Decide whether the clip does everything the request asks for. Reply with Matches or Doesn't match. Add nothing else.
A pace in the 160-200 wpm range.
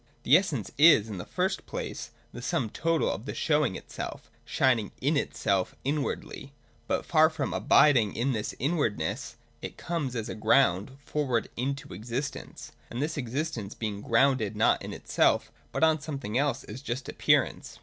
Matches